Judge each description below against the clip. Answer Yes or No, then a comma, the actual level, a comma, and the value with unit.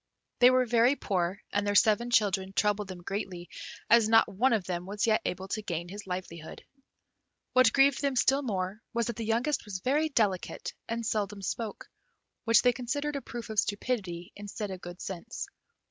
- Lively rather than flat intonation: No, average, 4.0 semitones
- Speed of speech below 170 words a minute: No, average, 185 wpm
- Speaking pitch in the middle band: No, high, 210 Hz